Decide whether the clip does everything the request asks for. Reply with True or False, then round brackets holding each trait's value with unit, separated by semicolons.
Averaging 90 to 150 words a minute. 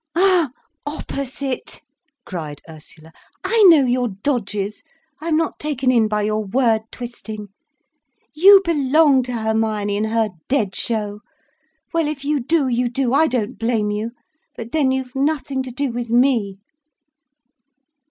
True (145 wpm)